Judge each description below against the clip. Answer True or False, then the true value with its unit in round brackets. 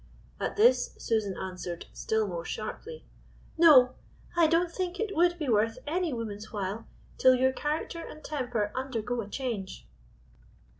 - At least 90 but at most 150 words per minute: True (145 wpm)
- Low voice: False (255 Hz)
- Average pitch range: False (7.6 semitones)